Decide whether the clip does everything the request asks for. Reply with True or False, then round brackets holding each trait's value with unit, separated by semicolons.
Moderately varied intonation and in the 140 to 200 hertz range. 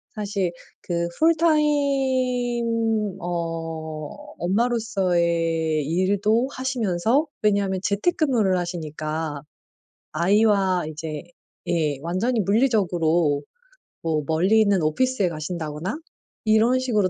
False (5.7 semitones; 190 Hz)